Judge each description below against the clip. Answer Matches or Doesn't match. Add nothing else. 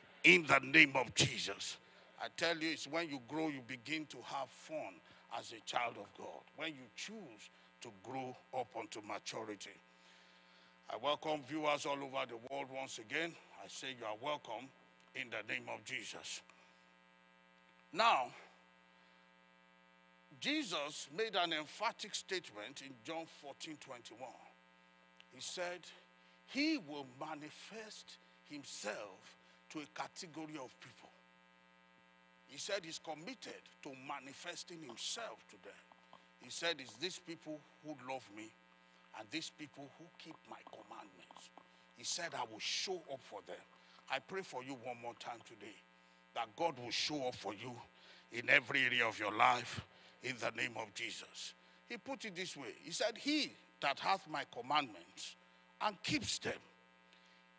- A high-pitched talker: Doesn't match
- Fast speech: Doesn't match